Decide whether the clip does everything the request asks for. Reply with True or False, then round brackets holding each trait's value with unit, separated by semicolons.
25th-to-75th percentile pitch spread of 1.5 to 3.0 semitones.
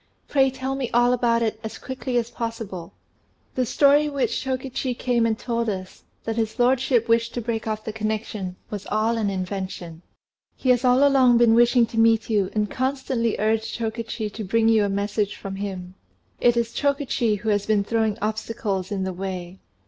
True (2.7 semitones)